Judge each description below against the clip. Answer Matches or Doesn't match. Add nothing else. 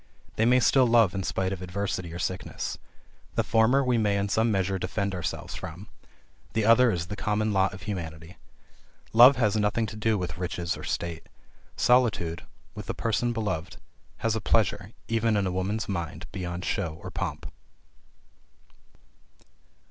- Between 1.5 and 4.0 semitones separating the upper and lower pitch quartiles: Matches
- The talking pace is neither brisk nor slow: Matches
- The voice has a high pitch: Doesn't match